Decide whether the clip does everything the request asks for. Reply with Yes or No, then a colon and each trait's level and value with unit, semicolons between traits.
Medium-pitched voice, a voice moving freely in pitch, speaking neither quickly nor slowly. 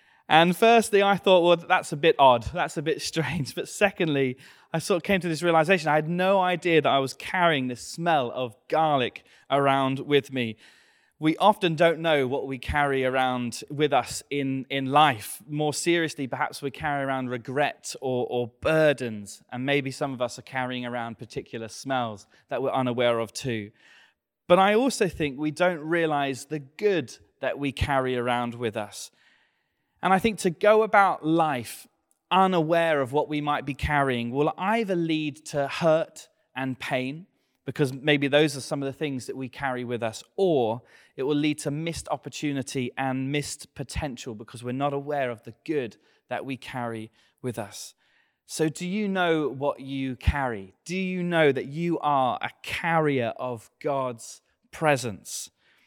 No: medium, 145 Hz; average, 4.5 semitones; average, 175 wpm